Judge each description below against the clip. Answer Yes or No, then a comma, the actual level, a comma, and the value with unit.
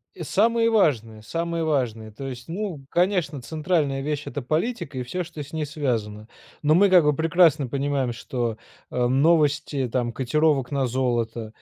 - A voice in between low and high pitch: Yes, medium, 145 Hz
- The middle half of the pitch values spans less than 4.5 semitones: No, average, 4.9 semitones